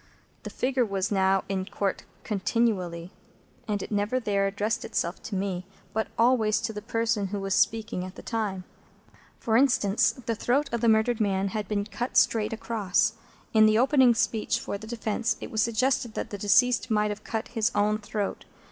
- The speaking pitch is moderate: No, high, 215 Hz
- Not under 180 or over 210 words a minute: Yes, average, 185 wpm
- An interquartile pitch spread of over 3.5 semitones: No, narrow, 2.4 semitones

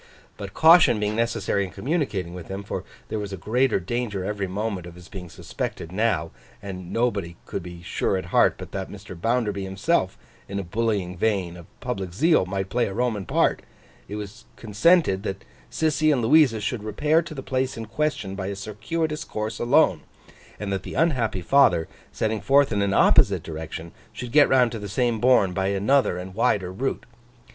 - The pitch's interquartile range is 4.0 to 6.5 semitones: Yes, average, 4.6 semitones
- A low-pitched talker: Yes, low, 105 Hz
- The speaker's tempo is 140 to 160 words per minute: No, average, 185 wpm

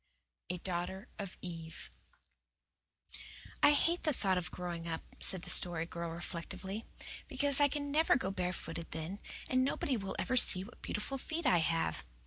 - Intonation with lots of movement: Yes, wide, 7.5 semitones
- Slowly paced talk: No, average, 160 wpm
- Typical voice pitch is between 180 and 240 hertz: Yes, high, 190 Hz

